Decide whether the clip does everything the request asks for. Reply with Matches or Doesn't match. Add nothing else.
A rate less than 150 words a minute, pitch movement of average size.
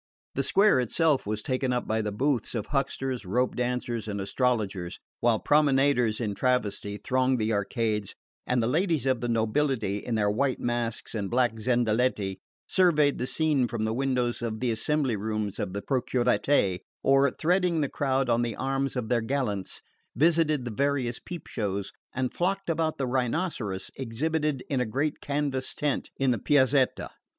Doesn't match